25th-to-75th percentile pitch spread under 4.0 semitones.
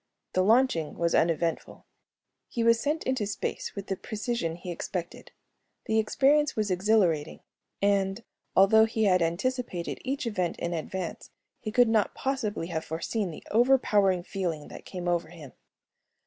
No: average, 4.9 semitones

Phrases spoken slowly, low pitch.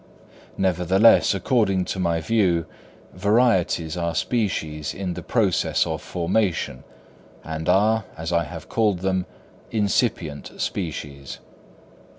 Yes: slow, 110 wpm; very low, 90 Hz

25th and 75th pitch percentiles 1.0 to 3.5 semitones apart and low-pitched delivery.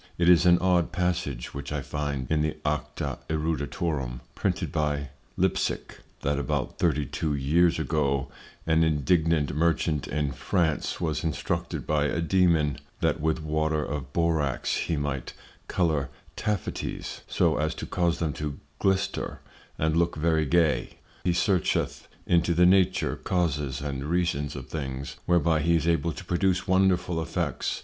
Yes: average, 2.9 semitones; very low, 80 Hz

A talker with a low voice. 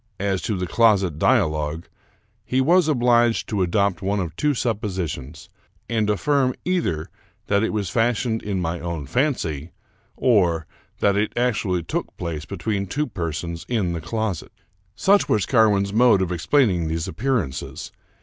Yes: low, 100 Hz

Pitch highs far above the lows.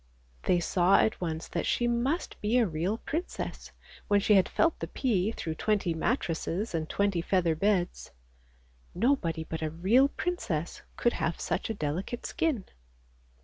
Yes: wide, 6.1 semitones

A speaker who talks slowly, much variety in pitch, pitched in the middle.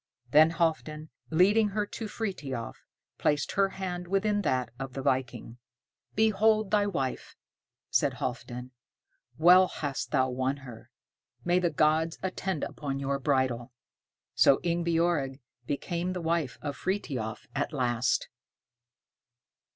Yes: slow, 120 wpm; wide, 5.8 semitones; medium, 155 Hz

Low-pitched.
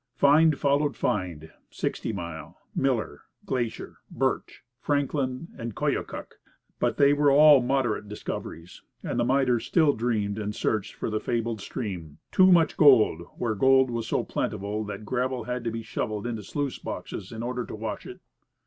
Yes: low, 120 Hz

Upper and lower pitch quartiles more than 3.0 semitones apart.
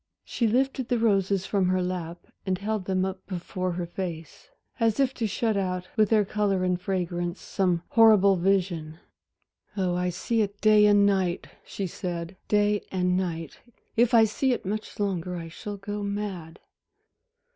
No: narrow, 2.6 semitones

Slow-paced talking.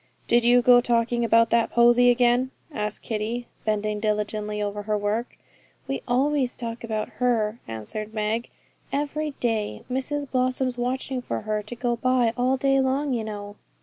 No: average, 160 wpm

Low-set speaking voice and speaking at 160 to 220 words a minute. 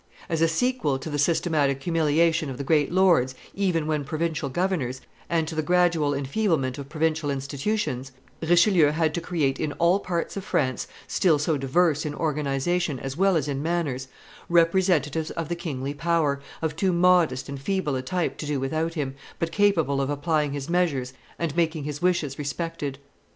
No: medium, 155 Hz; average, 175 wpm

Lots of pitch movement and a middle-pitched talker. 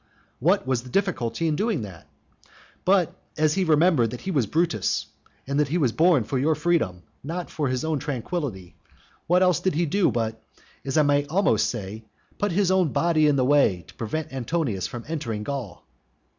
Yes: wide, 6.2 semitones; medium, 145 Hz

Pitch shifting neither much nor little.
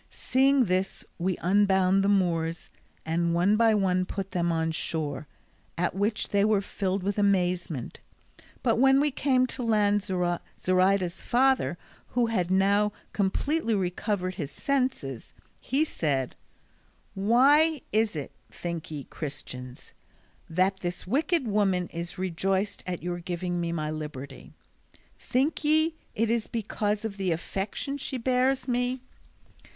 Yes: average, 4.9 semitones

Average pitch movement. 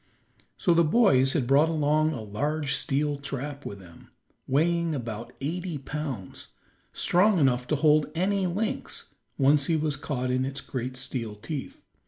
Yes: average, 3.7 semitones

